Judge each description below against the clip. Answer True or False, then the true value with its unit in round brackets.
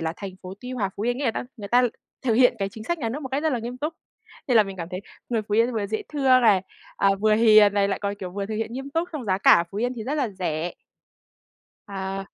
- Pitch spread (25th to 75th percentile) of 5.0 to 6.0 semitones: False (4.2 semitones)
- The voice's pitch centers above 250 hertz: False (220 Hz)